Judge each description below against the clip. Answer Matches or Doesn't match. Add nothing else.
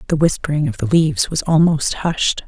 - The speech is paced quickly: Doesn't match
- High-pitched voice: Doesn't match